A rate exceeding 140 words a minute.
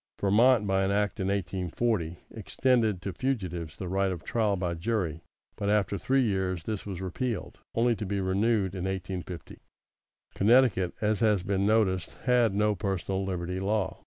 Yes: average, 160 wpm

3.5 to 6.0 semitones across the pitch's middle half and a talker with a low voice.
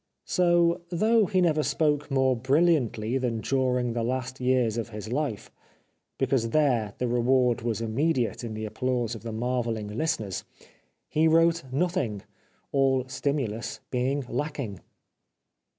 Yes: average, 4.4 semitones; low, 130 Hz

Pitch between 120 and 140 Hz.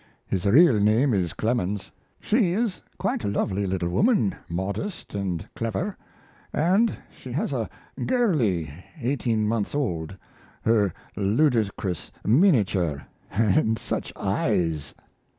No: low, 110 Hz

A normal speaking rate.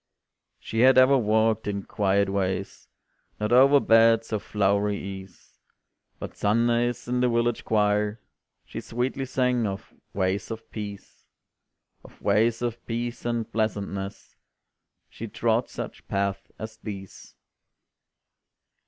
No: slow, 120 wpm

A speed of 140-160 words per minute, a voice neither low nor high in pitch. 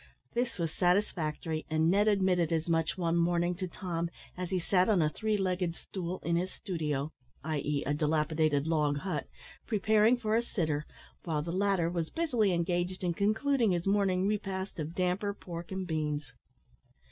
No: average, 170 wpm; medium, 175 Hz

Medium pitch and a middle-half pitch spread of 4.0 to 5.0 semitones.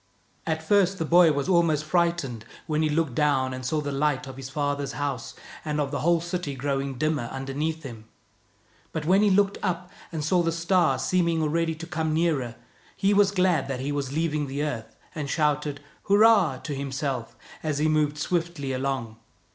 No: medium, 150 Hz; average, 3.6 semitones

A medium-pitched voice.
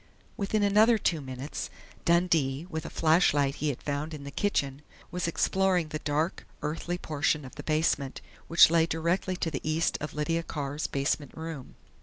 Yes: medium, 155 Hz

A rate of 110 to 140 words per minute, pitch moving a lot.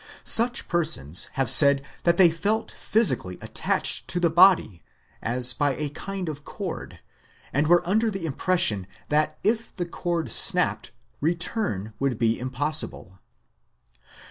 Yes: slow, 135 wpm; wide, 5.8 semitones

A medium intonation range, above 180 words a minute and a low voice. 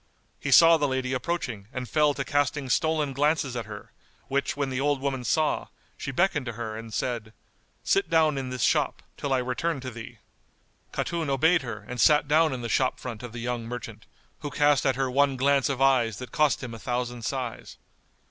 Yes: average, 3.1 semitones; fast, 205 wpm; low, 130 Hz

